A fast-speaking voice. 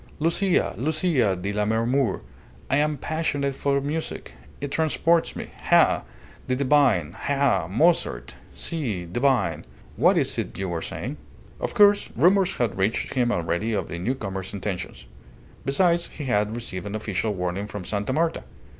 No: average, 145 wpm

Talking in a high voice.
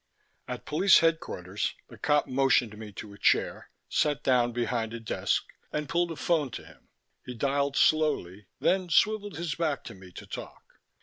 No: low, 135 Hz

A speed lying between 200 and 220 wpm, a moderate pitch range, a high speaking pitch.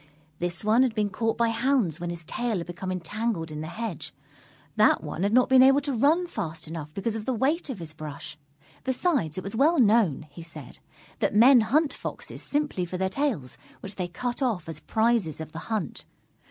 No: fast, 205 wpm; wide, 6.9 semitones; high, 215 Hz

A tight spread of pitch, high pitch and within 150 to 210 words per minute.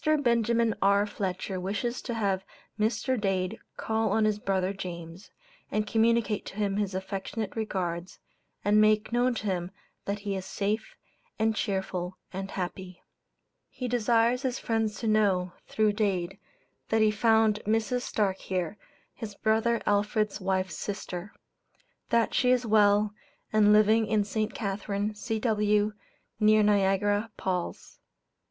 No: narrow, 2.3 semitones; high, 210 Hz; slow, 135 wpm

